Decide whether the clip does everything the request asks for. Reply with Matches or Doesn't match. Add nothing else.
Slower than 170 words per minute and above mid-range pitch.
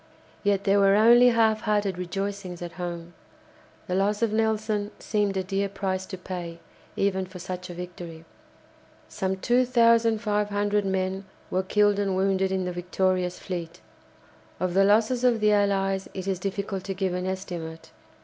Matches